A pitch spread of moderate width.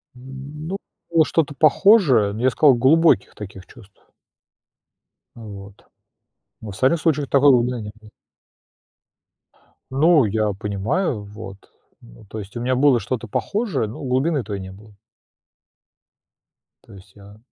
No: wide, 6.0 semitones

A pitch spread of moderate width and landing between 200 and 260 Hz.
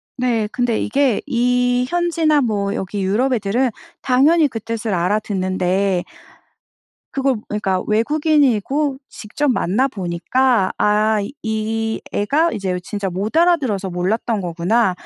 Yes: average, 4.9 semitones; high, 225 Hz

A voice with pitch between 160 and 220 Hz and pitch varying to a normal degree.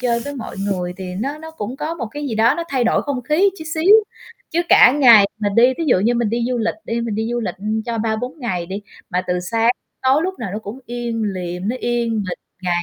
No: high, 235 Hz; average, 4.3 semitones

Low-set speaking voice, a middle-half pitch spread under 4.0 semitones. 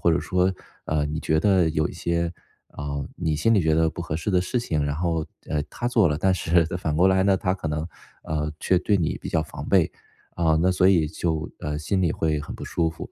Yes: very low, 80 Hz; average, 3.0 semitones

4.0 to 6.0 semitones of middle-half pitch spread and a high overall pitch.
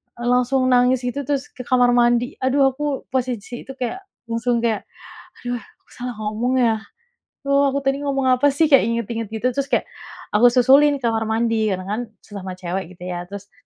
No: average, 3.2 semitones; high, 245 Hz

